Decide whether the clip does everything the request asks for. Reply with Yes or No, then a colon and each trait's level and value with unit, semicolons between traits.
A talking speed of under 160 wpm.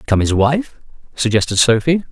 Yes: average, 140 wpm